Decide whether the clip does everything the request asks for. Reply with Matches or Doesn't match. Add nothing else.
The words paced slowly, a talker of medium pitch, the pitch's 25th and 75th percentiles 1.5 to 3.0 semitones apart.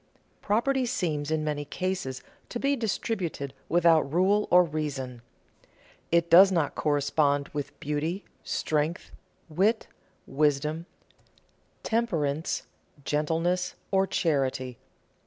Doesn't match